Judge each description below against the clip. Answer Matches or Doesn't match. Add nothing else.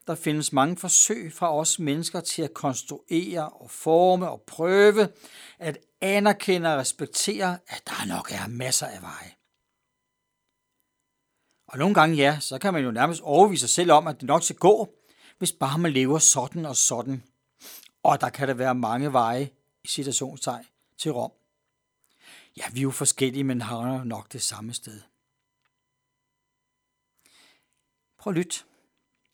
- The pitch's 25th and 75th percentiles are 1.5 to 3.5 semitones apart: Doesn't match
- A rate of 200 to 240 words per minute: Doesn't match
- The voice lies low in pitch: Doesn't match